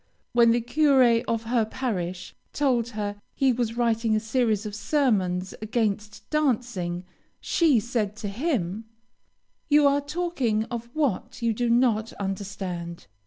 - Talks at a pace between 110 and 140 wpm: Yes, slow, 135 wpm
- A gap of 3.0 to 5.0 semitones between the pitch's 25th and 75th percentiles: Yes, average, 3.5 semitones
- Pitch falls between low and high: No, high, 230 Hz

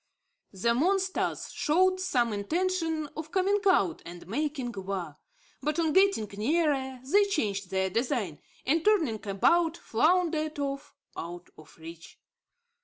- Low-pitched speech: No, very high, 285 Hz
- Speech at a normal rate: No, slow, 125 wpm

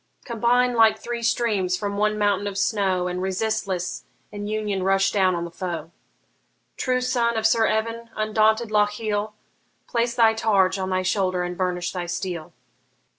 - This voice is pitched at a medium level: No, high, 205 Hz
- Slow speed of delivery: No, average, 160 wpm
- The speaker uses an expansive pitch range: No, average, 3.1 semitones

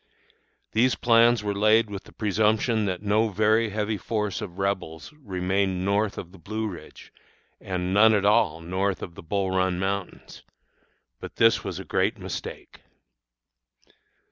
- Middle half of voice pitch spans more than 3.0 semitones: No, narrow, 2.6 semitones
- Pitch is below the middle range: Yes, low, 100 Hz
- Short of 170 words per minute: Yes, average, 150 wpm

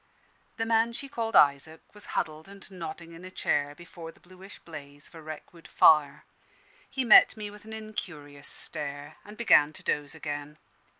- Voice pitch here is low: No, medium, 165 Hz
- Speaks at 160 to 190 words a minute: Yes, average, 180 wpm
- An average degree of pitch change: No, wide, 5.9 semitones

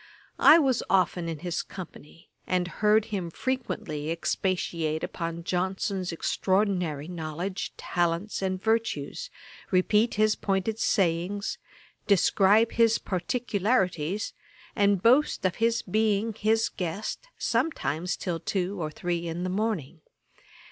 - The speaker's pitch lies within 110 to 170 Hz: No, high, 190 Hz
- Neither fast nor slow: No, slow, 115 wpm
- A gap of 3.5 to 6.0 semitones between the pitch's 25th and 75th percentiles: Yes, average, 4.1 semitones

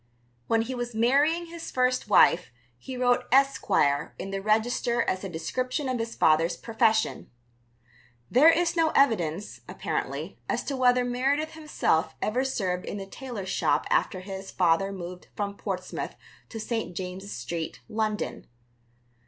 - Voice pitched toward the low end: No, high, 225 Hz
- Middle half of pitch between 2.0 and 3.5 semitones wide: No, wide, 5.4 semitones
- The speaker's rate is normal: Yes, average, 145 wpm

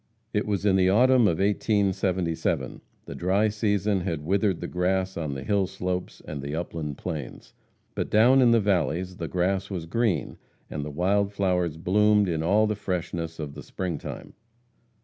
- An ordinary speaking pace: Yes, average, 175 wpm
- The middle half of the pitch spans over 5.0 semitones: No, average, 3.6 semitones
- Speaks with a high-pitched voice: No, very low, 95 Hz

